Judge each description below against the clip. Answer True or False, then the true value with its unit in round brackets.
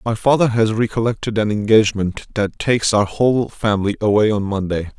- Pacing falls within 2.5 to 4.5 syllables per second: False (5.6 syllables/s)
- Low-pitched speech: True (110 Hz)